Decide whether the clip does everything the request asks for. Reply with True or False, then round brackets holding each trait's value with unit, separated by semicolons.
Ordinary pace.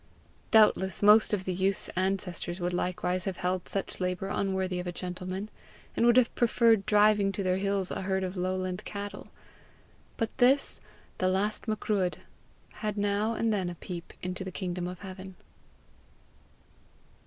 True (155 wpm)